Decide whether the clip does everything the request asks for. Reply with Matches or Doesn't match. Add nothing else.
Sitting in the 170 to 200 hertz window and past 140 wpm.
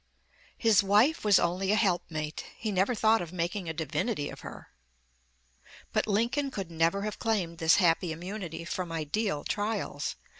Matches